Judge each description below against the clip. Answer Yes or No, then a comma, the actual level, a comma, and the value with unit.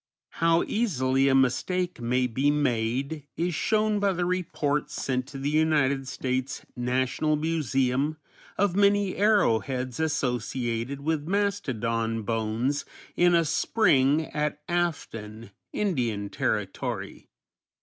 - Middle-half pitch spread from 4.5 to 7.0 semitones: Yes, average, 5.1 semitones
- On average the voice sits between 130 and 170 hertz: Yes, medium, 140 Hz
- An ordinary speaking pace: No, slow, 110 wpm